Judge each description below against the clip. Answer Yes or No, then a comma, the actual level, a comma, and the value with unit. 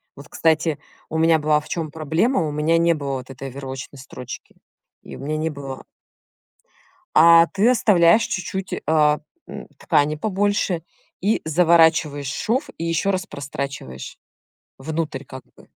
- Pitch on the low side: No, medium, 155 Hz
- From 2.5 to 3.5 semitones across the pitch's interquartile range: Yes, average, 3.1 semitones